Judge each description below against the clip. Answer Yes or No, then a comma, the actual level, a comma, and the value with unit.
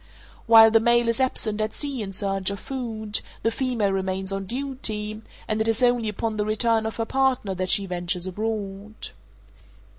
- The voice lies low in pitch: No, high, 215 Hz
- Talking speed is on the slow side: No, average, 180 wpm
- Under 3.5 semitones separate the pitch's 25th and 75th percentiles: Yes, average, 2.9 semitones